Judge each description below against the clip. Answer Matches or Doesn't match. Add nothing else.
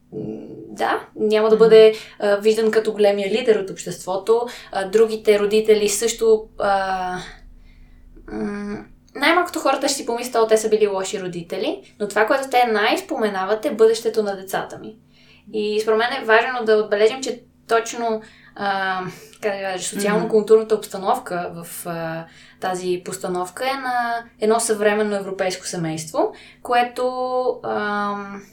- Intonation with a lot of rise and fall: Doesn't match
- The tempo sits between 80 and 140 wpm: Matches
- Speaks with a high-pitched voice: Matches